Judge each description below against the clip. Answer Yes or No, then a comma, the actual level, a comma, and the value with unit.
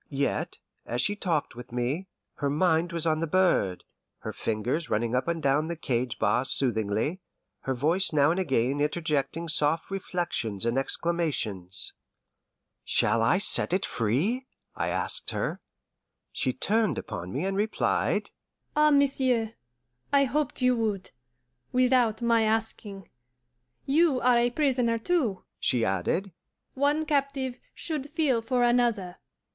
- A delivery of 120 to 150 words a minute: Yes, average, 140 wpm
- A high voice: No, medium, 180 Hz